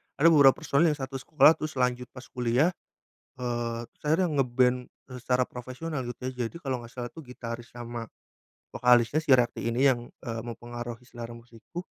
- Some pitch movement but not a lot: No, narrow, 2.2 semitones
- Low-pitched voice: Yes, low, 125 Hz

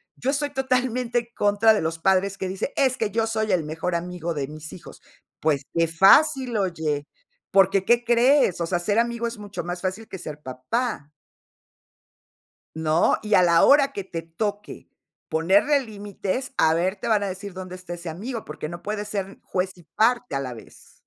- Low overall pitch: No, high, 195 Hz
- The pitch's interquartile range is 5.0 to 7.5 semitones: Yes, average, 5.3 semitones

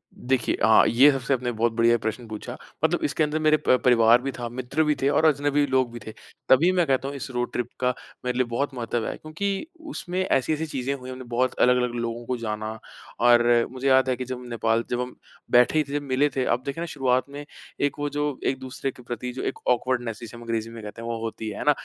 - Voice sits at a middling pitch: No, low, 125 Hz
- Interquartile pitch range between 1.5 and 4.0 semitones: Yes, average, 3.0 semitones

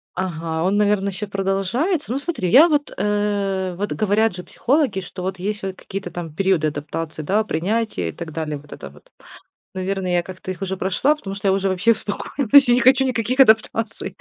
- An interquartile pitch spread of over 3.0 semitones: Yes, average, 3.5 semitones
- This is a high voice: Yes, high, 195 Hz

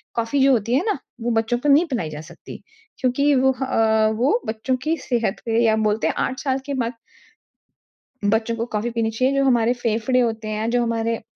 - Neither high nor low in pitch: No, high, 235 Hz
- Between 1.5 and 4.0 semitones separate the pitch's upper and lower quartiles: Yes, average, 2.9 semitones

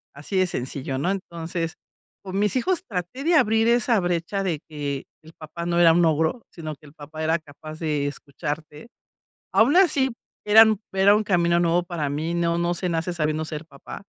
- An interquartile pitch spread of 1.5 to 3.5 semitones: No, average, 4.1 semitones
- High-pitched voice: No, medium, 170 Hz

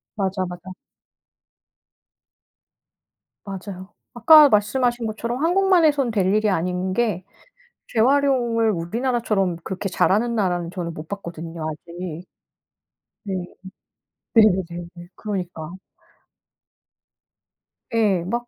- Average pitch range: Yes, average, 4.9 semitones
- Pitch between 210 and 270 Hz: No, high, 195 Hz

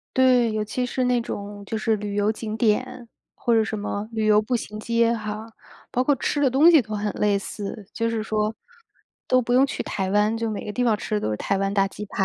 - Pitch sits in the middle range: No, high, 220 Hz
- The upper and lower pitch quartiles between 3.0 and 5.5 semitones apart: No, narrow, 2.5 semitones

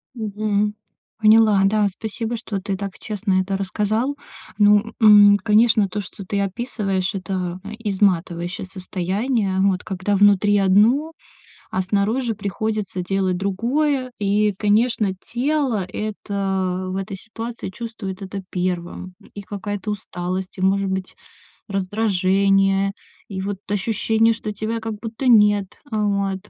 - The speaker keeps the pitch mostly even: Yes, narrow, 2.3 semitones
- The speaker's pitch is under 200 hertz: No, high, 205 Hz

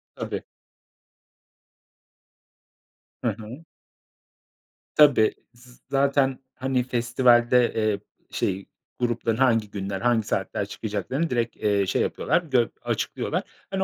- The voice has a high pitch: No, low, 120 Hz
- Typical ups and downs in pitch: Yes, average, 3.5 semitones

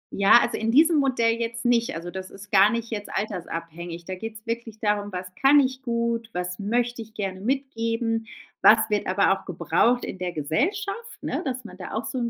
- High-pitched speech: Yes, high, 225 Hz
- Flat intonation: No, average, 3.8 semitones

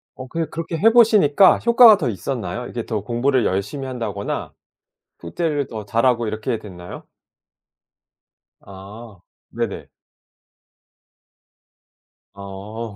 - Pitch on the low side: Yes, low, 120 Hz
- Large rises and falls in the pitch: Yes, wide, 6.1 semitones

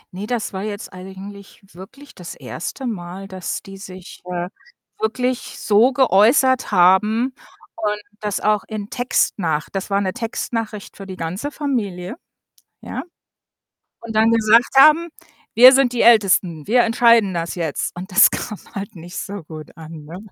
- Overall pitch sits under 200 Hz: No, high, 205 Hz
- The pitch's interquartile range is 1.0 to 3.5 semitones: No, average, 4.0 semitones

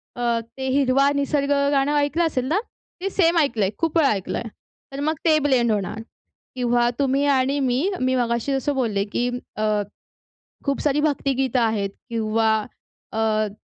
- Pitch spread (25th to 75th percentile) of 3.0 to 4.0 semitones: Yes, average, 3.6 semitones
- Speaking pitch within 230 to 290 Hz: Yes, very high, 260 Hz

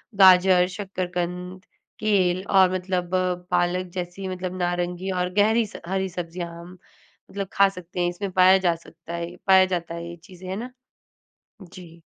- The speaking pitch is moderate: Yes, medium, 180 Hz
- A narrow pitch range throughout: Yes, narrow, 1.3 semitones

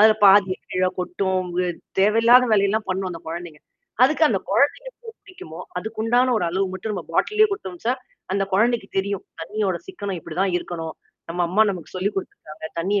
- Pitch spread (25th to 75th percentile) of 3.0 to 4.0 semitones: Yes, average, 3.4 semitones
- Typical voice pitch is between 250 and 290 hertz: No, high, 195 Hz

